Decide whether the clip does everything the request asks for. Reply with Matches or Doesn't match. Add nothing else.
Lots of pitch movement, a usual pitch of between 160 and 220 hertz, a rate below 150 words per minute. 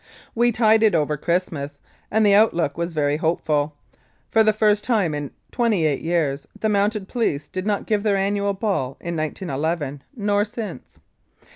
Doesn't match